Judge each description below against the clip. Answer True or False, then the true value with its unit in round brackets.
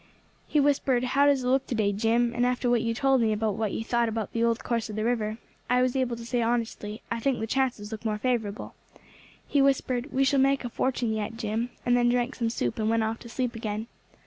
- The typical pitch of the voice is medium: False (235 Hz)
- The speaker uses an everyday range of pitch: False (2.3 semitones)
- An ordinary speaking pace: False (250 wpm)